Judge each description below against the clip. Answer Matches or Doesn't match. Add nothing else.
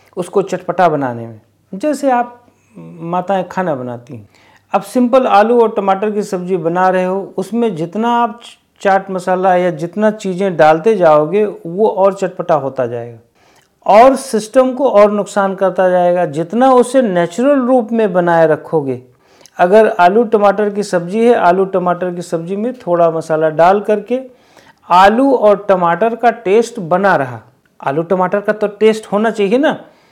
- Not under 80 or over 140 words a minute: Doesn't match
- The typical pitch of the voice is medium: Doesn't match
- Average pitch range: Matches